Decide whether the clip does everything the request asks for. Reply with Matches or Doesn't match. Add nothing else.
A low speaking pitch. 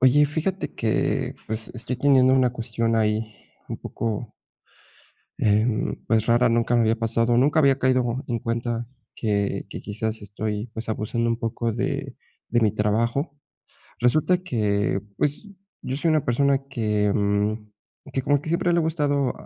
Matches